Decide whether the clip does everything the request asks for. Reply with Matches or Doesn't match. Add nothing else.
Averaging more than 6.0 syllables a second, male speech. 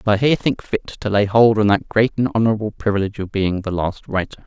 Matches